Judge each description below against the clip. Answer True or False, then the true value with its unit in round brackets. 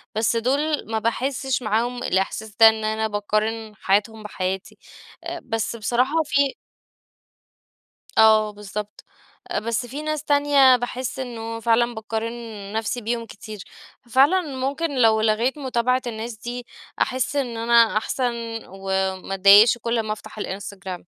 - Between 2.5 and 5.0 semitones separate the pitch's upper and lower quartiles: True (3.0 semitones)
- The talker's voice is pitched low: False (230 Hz)